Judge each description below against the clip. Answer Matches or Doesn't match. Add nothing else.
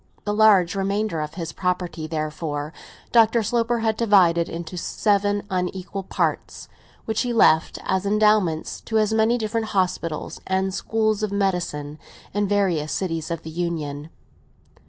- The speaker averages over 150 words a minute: Doesn't match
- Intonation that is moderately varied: Matches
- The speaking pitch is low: Doesn't match